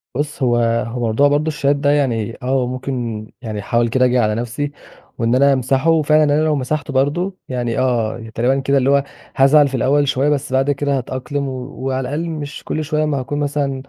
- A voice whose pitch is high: No, low, 135 Hz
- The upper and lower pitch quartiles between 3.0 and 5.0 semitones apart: No, narrow, 2.5 semitones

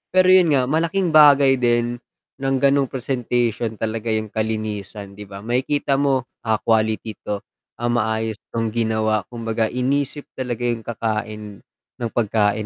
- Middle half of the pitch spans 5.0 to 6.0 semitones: No, average, 3.4 semitones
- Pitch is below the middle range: Yes, low, 120 Hz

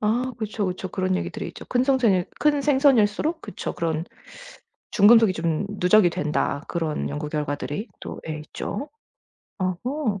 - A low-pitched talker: No, high, 200 Hz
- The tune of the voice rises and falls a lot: Yes, wide, 6.9 semitones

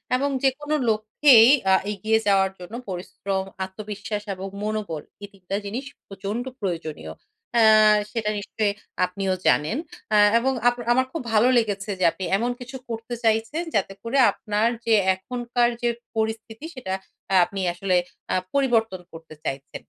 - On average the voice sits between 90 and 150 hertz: No, high, 215 Hz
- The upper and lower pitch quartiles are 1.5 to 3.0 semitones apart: No, average, 3.7 semitones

